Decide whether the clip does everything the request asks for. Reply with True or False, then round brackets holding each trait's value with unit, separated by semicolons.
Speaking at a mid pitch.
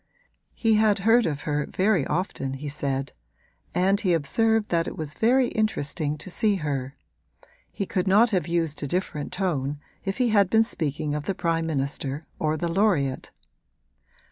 True (170 Hz)